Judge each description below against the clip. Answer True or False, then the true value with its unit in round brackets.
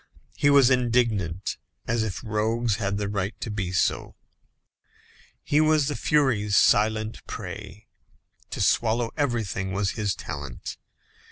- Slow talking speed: True (125 wpm)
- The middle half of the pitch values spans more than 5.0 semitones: False (3.3 semitones)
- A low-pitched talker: True (110 Hz)